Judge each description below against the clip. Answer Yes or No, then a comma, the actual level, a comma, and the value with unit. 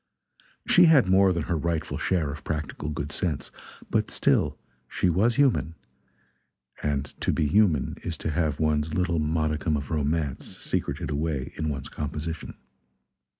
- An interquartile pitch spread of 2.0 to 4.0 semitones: Yes, narrow, 2.6 semitones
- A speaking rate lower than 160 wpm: Yes, average, 150 wpm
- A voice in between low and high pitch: No, very low, 80 Hz